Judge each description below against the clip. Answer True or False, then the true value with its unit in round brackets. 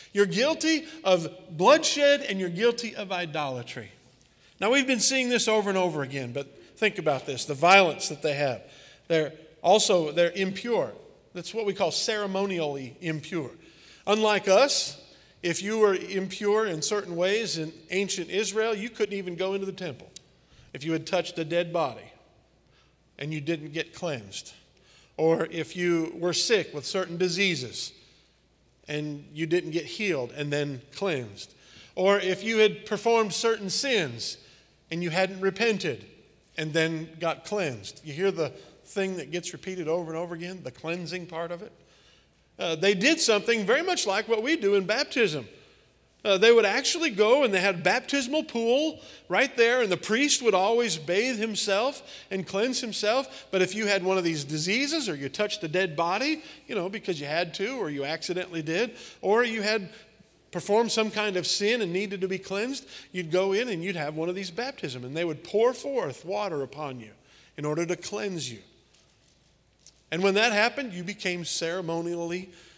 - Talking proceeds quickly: False (180 wpm)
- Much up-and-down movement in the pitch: False (4.5 semitones)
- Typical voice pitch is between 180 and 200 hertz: True (185 Hz)